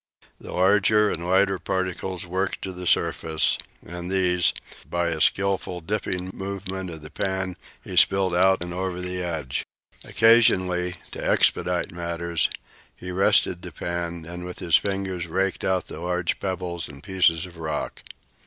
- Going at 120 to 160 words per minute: Yes, average, 155 wpm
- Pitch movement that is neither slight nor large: No, narrow, 1.6 semitones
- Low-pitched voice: Yes, very low, 90 Hz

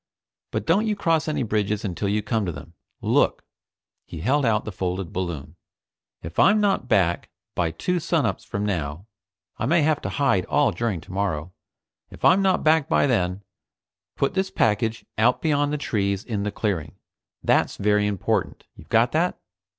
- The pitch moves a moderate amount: No, wide, 7.9 semitones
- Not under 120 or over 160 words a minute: No, average, 175 wpm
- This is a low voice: Yes, low, 105 Hz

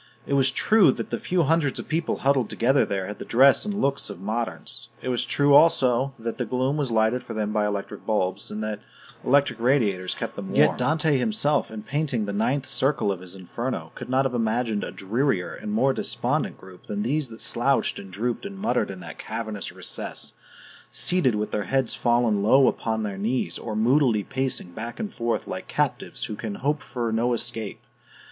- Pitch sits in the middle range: No, low, 120 Hz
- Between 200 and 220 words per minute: Yes, fast, 205 wpm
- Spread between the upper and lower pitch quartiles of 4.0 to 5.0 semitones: Yes, average, 4.5 semitones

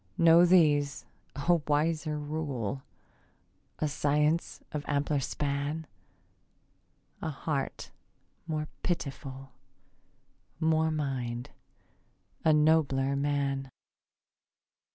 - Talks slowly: Yes, slow, 75 wpm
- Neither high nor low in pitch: Yes, medium, 145 Hz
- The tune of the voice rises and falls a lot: No, narrow, 2.3 semitones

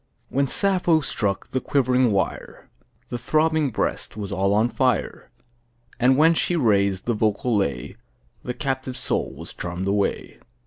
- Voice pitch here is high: No, low, 125 Hz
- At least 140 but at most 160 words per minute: Yes, average, 150 wpm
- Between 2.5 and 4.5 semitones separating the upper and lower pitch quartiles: No, wide, 5.5 semitones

